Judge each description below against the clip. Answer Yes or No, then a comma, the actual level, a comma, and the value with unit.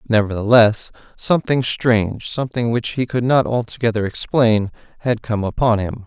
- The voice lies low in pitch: Yes, low, 115 Hz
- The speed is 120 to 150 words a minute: Yes, average, 140 wpm